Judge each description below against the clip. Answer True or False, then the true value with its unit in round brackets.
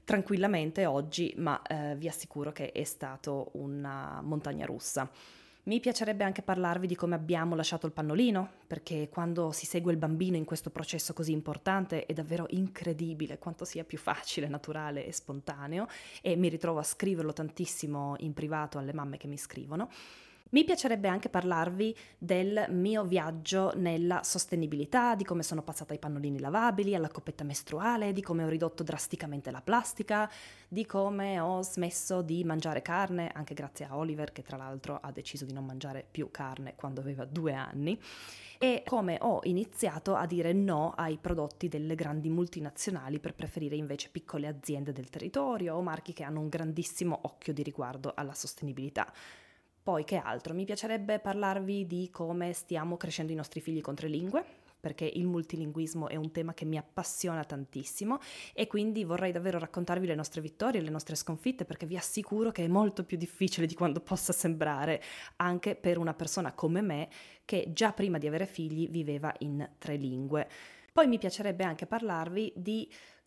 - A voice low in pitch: False (165 Hz)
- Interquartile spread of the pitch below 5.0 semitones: True (3.6 semitones)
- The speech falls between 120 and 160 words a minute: False (170 wpm)